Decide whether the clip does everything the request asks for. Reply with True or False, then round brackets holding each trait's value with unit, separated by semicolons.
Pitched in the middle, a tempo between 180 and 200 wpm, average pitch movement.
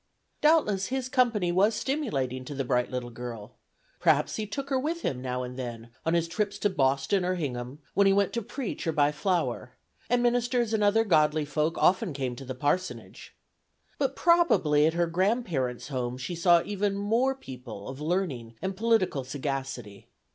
False (170 Hz; 185 wpm; 8.1 semitones)